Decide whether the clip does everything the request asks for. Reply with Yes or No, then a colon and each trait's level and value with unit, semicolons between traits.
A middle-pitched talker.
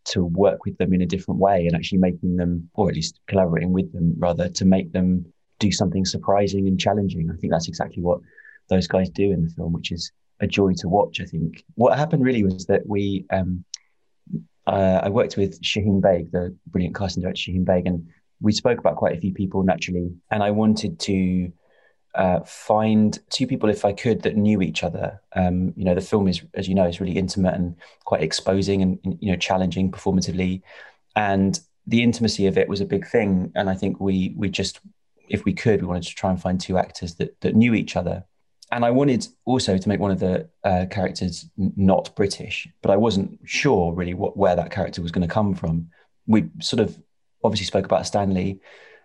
No: very low, 95 Hz